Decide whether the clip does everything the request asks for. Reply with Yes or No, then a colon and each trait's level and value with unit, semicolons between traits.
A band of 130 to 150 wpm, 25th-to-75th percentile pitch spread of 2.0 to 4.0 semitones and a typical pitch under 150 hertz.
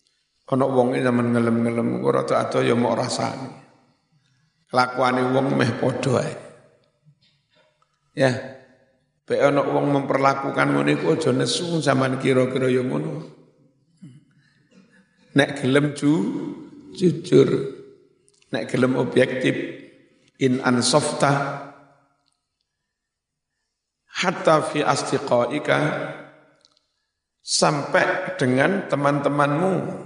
No: average, 90 wpm; average, 3.2 semitones; medium, 140 Hz